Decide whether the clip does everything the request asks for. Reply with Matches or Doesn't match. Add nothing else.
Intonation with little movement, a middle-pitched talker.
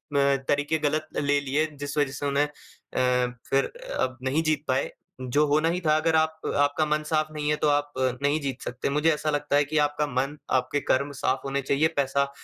Matches